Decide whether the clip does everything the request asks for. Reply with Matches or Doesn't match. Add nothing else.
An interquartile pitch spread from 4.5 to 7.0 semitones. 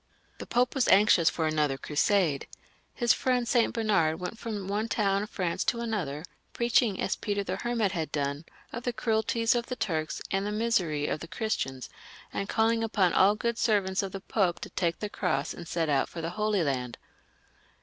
Matches